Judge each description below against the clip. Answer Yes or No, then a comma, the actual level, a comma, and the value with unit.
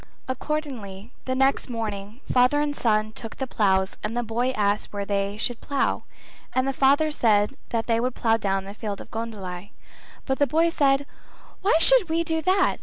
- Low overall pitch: No, high, 235 Hz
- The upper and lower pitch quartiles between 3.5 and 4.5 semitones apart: No, average, 5.1 semitones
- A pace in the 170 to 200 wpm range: Yes, average, 190 wpm